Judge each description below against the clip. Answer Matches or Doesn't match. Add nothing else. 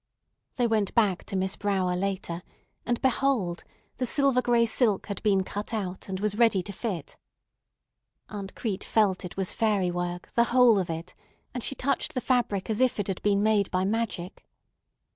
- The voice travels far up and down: Doesn't match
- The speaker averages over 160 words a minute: Matches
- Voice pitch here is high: Matches